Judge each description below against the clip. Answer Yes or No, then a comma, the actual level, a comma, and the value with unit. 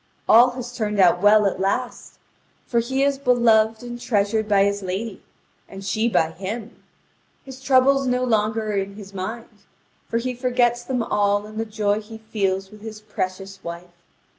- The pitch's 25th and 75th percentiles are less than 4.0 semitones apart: Yes, average, 3.2 semitones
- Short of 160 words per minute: No, average, 175 wpm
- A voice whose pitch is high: Yes, high, 215 Hz